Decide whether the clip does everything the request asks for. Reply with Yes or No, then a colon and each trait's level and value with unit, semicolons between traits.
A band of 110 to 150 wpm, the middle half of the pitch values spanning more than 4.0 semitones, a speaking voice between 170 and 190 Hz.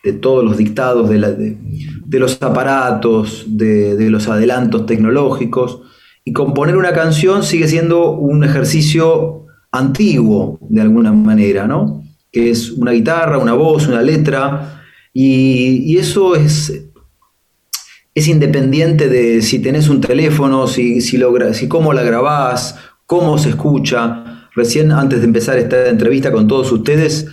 No: average, 145 wpm; average, 4.6 semitones; low, 135 Hz